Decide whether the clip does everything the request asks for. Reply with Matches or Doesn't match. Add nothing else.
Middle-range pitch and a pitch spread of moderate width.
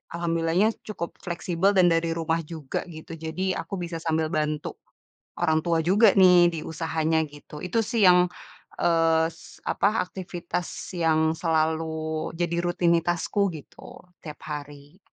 Doesn't match